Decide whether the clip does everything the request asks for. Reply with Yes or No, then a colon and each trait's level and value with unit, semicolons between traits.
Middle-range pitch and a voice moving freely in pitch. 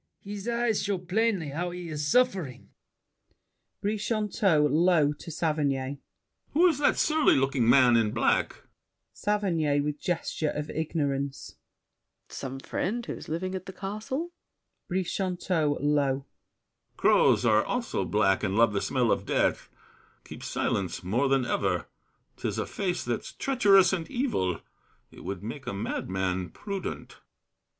Yes: medium, 155 Hz; wide, 7.0 semitones